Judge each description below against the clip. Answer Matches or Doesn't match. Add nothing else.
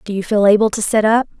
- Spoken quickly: Matches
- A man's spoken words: Doesn't match